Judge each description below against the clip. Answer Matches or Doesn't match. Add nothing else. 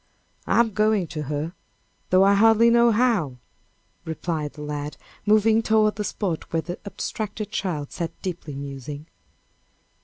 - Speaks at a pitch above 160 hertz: Matches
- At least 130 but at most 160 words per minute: Matches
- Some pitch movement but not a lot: Doesn't match